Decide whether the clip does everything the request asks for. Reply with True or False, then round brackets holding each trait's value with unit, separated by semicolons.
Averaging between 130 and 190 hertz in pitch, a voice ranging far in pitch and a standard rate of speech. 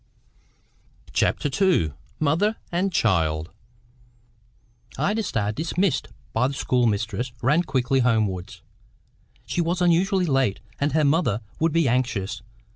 False (135 Hz; 7.3 semitones; 115 wpm)